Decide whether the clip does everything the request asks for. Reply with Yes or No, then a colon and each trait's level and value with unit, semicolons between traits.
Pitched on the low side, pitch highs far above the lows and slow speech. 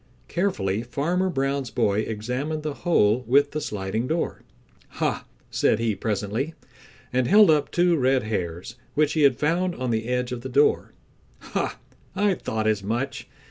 No: low, 130 Hz; wide, 5.7 semitones; average, 160 wpm